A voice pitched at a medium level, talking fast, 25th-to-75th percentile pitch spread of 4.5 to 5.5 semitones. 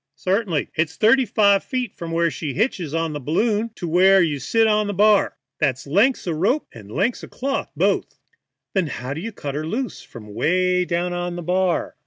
Yes: medium, 180 Hz; fast, 210 wpm; average, 5.0 semitones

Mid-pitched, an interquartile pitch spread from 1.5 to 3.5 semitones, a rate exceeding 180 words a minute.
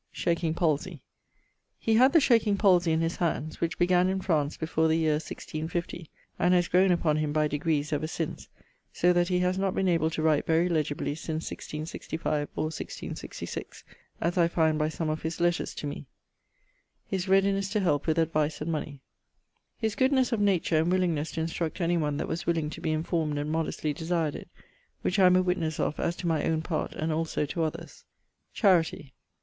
Yes: medium, 165 Hz; narrow, 2.5 semitones; average, 195 wpm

